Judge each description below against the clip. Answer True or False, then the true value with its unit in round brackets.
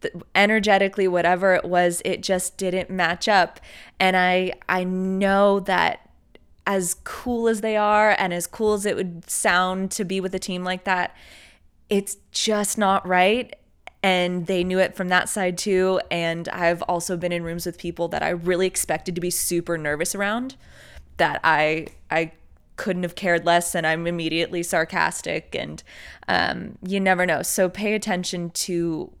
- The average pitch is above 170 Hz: True (185 Hz)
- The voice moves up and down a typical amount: False (2.2 semitones)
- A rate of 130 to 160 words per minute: False (170 wpm)